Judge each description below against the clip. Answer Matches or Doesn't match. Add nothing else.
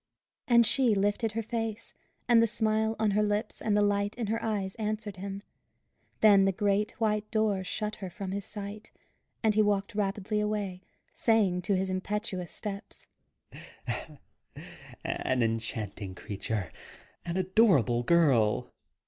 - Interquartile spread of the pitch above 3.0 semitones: Doesn't match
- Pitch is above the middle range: Matches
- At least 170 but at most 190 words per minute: Doesn't match